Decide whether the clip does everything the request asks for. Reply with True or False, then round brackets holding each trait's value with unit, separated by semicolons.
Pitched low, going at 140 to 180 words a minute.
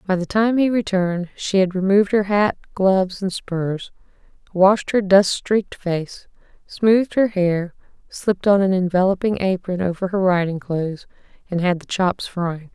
False (190 Hz; 165 wpm)